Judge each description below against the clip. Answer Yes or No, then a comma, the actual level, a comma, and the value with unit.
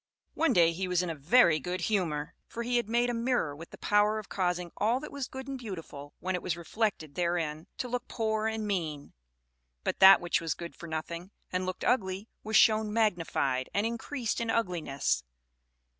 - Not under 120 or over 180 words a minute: No, average, 200 wpm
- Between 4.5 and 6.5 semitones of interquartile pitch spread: Yes, average, 5.1 semitones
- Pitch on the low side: No, high, 190 Hz